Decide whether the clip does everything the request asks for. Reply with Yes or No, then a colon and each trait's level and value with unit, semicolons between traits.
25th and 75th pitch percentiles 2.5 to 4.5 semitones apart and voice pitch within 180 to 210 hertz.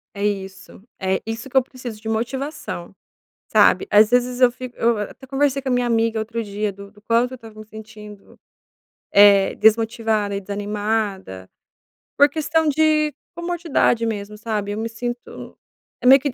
No: average, 3.4 semitones; high, 225 Hz